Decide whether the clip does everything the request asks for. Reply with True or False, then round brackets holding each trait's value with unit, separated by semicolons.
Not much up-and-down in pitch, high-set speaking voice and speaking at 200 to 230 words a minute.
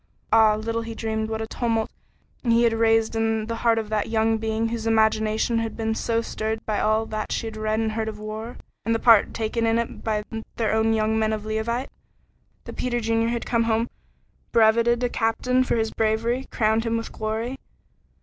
True (0.8 semitones; 225 Hz; 205 wpm)